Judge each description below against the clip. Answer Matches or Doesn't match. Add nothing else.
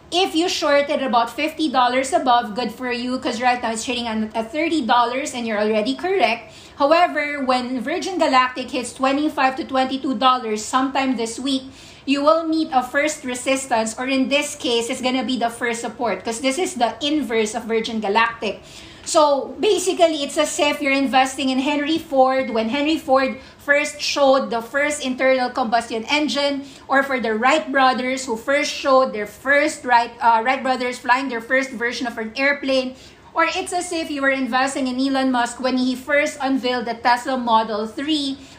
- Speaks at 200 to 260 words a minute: Doesn't match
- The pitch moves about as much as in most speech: Matches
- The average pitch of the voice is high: Matches